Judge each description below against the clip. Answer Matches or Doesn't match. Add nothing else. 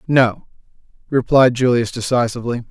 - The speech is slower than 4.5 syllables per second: Doesn't match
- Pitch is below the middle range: Matches